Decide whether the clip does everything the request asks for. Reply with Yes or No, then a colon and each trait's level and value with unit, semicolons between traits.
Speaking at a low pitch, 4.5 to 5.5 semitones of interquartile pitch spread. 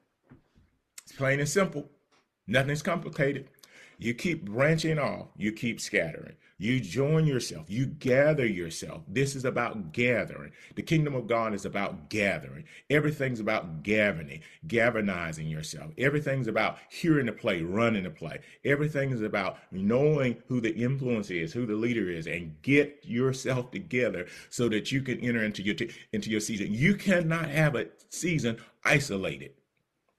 Yes: low, 125 Hz; average, 5.1 semitones